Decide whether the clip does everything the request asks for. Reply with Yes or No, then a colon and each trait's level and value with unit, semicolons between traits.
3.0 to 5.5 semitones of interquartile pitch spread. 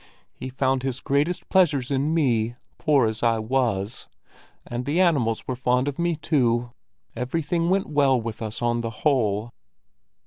Yes: average, 3.8 semitones